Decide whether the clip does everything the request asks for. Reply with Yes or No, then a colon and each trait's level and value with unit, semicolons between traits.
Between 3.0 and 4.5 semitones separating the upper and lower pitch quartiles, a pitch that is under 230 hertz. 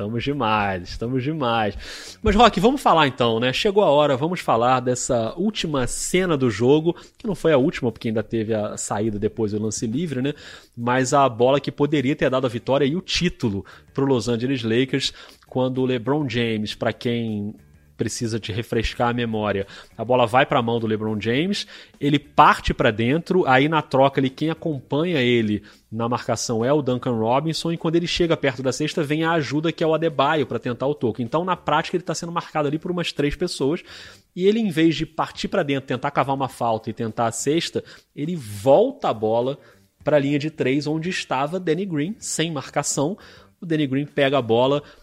No: average, 5.0 semitones; low, 135 Hz